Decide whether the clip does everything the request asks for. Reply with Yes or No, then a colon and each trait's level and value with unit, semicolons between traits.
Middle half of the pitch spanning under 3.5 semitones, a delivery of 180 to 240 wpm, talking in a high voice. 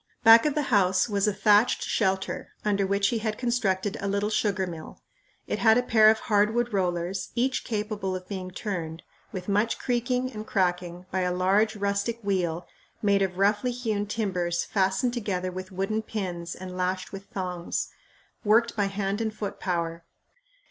No: average, 2.9 semitones; average, 170 wpm; high, 200 Hz